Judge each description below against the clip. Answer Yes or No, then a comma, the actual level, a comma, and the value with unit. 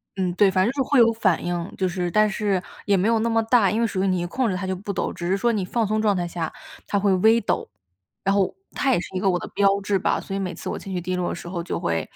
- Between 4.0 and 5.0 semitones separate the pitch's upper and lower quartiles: No, average, 3.0 semitones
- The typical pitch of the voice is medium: No, high, 195 Hz